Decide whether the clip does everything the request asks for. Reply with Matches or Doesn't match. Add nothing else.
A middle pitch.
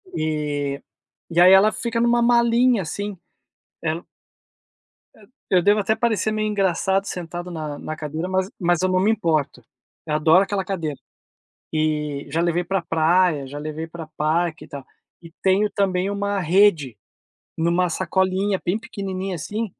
Matches